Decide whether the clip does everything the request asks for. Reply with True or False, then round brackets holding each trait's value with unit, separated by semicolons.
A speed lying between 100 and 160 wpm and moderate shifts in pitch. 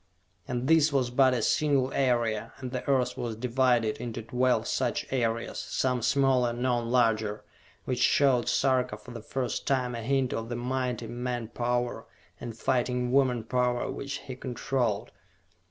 False (155 wpm; 1.6 semitones)